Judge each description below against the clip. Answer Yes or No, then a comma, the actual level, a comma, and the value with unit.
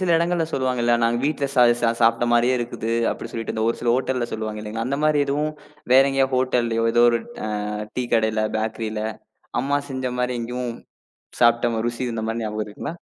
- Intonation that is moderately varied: No, narrow, 2.3 semitones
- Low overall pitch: Yes, low, 120 Hz